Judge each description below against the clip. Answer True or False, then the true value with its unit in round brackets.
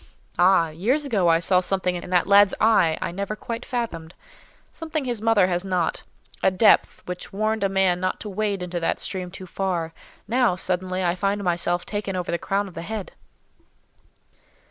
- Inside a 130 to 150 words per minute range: False (175 wpm)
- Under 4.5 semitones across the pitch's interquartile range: True (2.9 semitones)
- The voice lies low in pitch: False (190 Hz)